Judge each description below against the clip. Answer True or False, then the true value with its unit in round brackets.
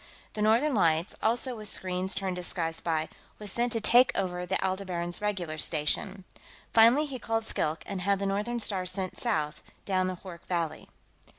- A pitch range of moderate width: True (3.9 semitones)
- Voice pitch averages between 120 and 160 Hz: False (190 Hz)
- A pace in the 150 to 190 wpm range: True (185 wpm)